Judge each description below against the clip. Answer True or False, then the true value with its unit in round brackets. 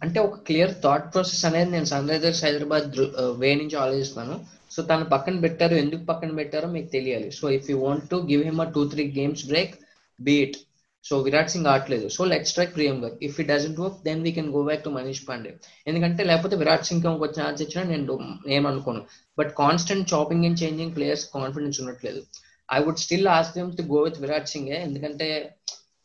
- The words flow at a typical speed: False (185 wpm)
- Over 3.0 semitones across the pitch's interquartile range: False (2.6 semitones)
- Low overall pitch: False (150 Hz)